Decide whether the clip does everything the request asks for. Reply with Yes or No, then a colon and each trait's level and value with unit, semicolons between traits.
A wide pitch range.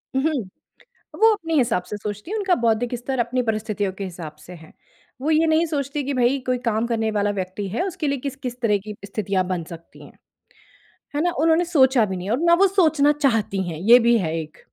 Yes: wide, 6.5 semitones